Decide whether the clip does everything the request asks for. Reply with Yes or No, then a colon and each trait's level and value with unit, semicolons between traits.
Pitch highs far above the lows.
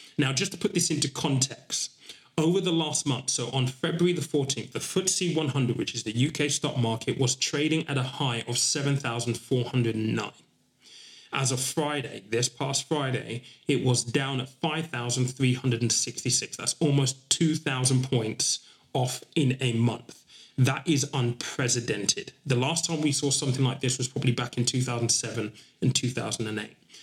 No: average, 3.4 semitones